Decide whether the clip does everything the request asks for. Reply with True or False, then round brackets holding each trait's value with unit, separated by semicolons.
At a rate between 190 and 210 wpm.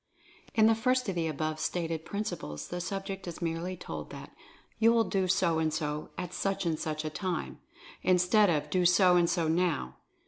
True (200 wpm)